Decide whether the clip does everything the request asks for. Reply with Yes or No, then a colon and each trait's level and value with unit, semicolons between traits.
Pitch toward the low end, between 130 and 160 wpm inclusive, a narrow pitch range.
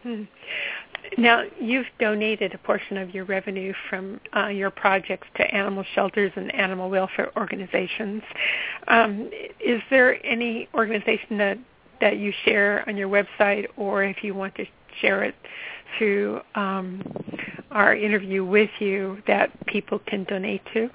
No: high, 205 Hz; average, 140 wpm; narrow, 2.0 semitones